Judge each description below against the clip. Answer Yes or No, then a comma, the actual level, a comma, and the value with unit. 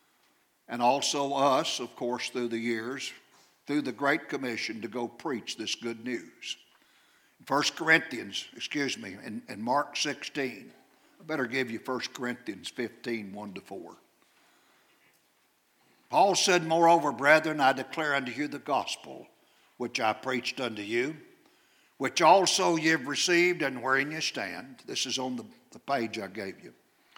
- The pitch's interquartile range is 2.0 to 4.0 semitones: No, average, 4.7 semitones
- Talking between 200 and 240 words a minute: No, average, 150 wpm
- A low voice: Yes, low, 130 Hz